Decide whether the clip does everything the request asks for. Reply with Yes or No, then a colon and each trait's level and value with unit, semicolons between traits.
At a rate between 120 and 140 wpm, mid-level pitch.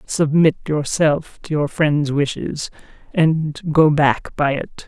Yes: slow, 135 wpm; medium, 150 Hz